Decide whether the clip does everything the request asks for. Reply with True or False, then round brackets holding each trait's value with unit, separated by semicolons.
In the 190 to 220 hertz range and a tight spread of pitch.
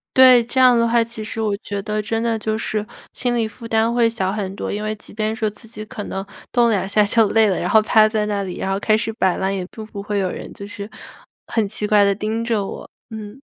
True (215 Hz; 1.9 semitones)